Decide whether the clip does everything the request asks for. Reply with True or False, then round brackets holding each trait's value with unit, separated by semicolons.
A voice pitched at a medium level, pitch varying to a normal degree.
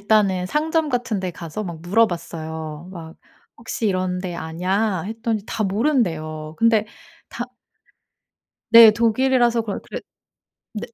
False (205 Hz; 5.0 semitones)